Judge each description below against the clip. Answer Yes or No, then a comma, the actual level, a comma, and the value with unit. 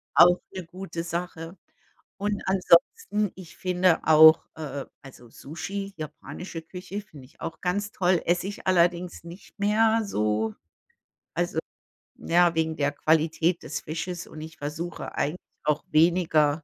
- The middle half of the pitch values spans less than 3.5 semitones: Yes, average, 2.9 semitones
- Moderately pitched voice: Yes, medium, 170 Hz